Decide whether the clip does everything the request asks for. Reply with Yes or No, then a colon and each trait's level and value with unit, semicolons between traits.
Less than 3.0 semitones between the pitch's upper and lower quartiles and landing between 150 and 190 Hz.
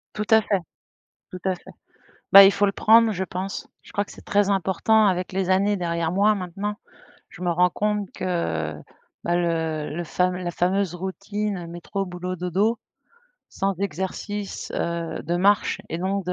Yes: narrow, 2.4 semitones; medium, 185 Hz